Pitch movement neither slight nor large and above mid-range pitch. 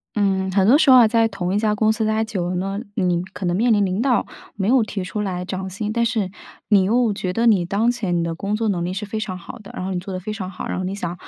Yes: average, 3.0 semitones; high, 200 Hz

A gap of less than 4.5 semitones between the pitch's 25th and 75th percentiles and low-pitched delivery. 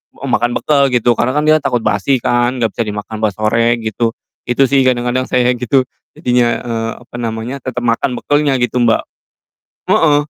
Yes: narrow, 2.4 semitones; low, 120 Hz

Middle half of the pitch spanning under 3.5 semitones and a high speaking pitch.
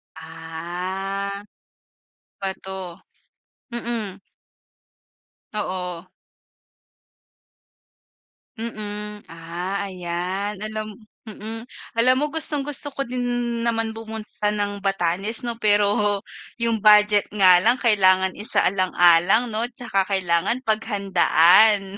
Yes: average, 3.0 semitones; high, 205 Hz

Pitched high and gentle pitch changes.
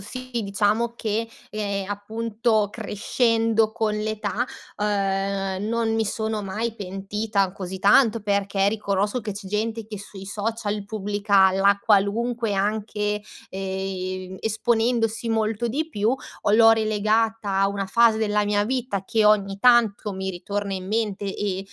Yes: high, 210 Hz; narrow, 2.0 semitones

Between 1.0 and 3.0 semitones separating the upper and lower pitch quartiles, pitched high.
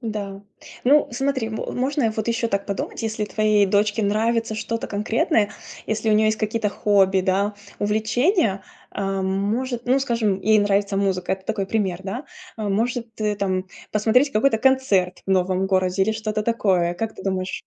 Yes: average, 2.7 semitones; high, 215 Hz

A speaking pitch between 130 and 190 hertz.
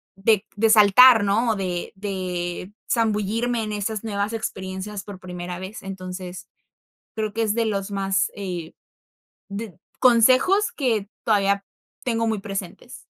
No: high, 205 Hz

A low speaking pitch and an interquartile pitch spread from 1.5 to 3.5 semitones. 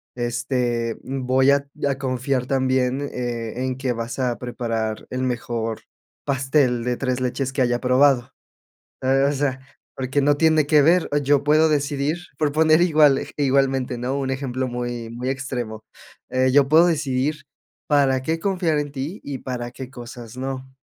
Yes: low, 130 Hz; narrow, 2.4 semitones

